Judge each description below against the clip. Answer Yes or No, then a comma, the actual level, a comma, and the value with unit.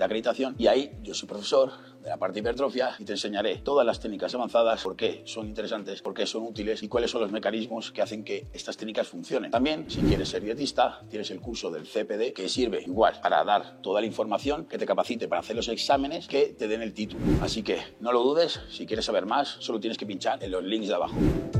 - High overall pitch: No, low, 115 Hz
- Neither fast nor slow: No, fast, 240 wpm